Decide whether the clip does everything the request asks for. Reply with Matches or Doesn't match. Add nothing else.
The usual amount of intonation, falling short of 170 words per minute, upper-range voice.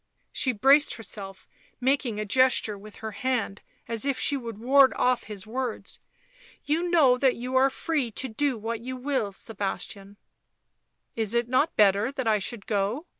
Doesn't match